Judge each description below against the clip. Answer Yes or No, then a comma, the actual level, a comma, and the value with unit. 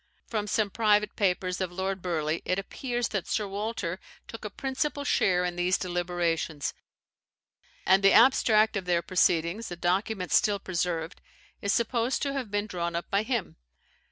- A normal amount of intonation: Yes, average, 3.6 semitones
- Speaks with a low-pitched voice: No, high, 195 Hz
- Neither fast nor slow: Yes, average, 160 wpm